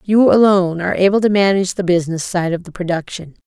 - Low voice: No, medium, 185 Hz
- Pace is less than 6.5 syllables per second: No, 6.7 syllables/s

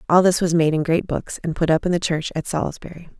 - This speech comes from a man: No, female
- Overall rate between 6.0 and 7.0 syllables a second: Yes, 6.2 syllables/s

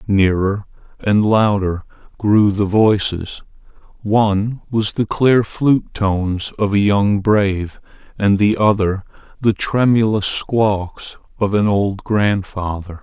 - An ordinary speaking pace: No, slow, 115 wpm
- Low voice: Yes, low, 100 Hz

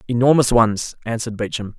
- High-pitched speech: No, low, 115 Hz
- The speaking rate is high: No, slow, 135 wpm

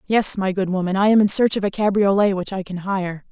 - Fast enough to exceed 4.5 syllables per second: Yes, 5.7 syllables/s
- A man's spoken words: No, female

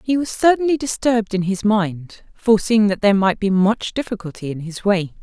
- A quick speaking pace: No, average, 195 wpm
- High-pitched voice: Yes, high, 205 Hz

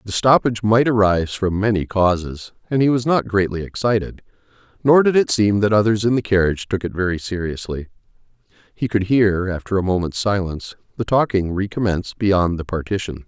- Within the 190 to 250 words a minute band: No, average, 175 wpm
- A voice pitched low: Yes, low, 100 Hz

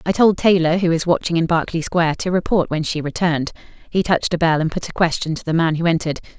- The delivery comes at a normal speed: No, fast, 255 wpm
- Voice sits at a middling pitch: Yes, medium, 165 Hz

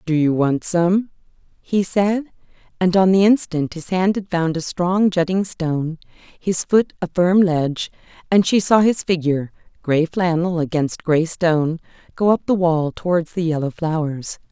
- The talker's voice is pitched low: No, medium, 175 Hz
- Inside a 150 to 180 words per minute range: Yes, average, 165 wpm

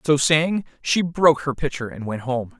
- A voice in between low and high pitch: Yes, medium, 145 Hz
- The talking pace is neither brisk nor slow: No, fast, 210 wpm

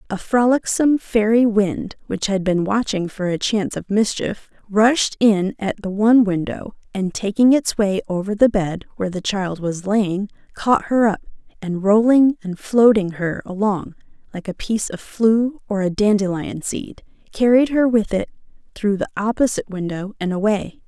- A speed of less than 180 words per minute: Yes, average, 170 wpm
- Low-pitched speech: No, high, 205 Hz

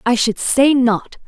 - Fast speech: No, average, 190 wpm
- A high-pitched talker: Yes, high, 240 Hz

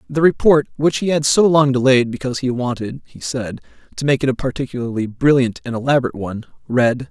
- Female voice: No, male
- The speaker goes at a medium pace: Yes, average, 195 wpm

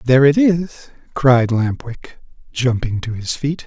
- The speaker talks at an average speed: Yes, average, 165 wpm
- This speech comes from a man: Yes, male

